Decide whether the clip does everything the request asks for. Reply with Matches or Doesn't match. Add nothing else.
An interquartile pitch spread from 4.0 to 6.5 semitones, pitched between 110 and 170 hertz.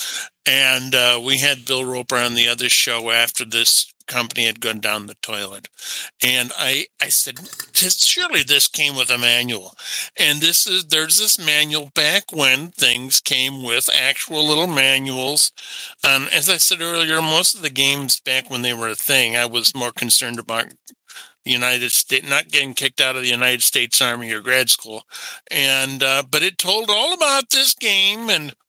Matches